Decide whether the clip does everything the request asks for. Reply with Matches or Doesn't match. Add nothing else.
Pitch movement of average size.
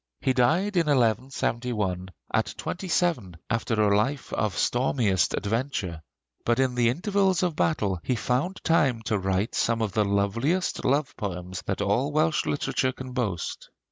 Doesn't match